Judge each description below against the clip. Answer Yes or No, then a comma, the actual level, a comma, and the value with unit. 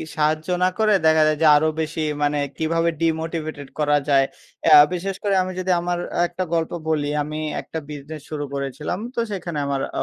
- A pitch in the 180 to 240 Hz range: No, medium, 155 Hz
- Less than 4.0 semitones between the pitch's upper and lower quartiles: Yes, narrow, 2.4 semitones